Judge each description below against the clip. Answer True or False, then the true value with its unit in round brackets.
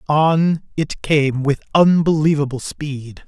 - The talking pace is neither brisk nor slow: False (110 wpm)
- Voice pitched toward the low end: False (150 Hz)